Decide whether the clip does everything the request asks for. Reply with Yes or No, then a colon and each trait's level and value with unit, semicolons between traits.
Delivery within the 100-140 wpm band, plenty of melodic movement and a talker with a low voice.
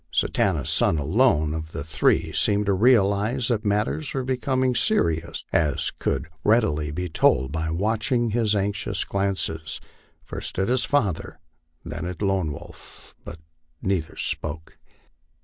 Yes: slow, 135 wpm; wide, 6.3 semitones; low, 100 Hz